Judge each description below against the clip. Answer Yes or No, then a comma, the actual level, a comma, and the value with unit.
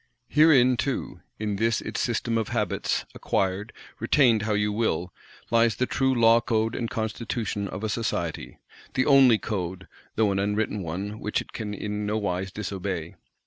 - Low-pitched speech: Yes, low, 105 Hz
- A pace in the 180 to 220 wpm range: No, average, 160 wpm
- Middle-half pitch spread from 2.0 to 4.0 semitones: Yes, average, 2.8 semitones